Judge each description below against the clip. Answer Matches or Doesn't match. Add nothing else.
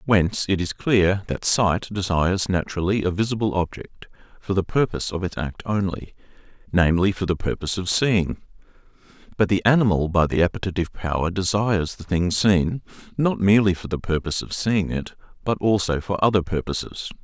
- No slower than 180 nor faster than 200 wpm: Doesn't match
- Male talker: Matches